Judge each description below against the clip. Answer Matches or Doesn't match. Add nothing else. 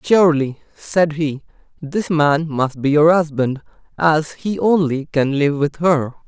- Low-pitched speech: Doesn't match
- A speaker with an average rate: Matches